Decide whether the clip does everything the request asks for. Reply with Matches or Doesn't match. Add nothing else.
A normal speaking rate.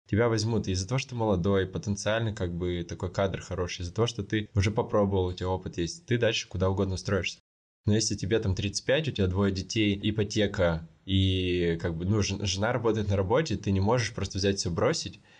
Doesn't match